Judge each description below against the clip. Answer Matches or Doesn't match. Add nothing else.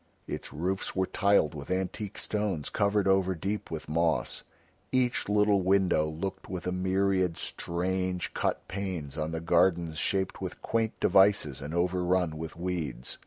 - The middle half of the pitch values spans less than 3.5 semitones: Matches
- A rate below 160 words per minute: Matches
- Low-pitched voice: Matches